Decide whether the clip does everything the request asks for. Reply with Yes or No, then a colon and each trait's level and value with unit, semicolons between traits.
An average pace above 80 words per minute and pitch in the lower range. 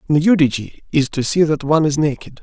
No: average, 200 wpm; medium, 150 Hz